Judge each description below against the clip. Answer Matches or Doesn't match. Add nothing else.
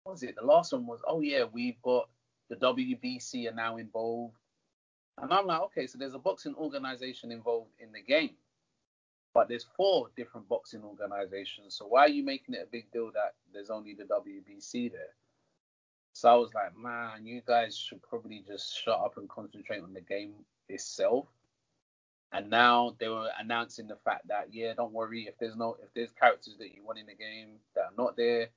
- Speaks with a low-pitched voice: Matches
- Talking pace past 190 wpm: Matches